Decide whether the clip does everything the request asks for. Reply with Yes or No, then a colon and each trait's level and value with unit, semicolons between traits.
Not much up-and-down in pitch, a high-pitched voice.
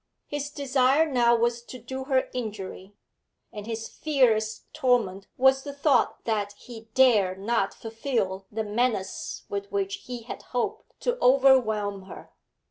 No: average, 4.3 semitones; high, 235 Hz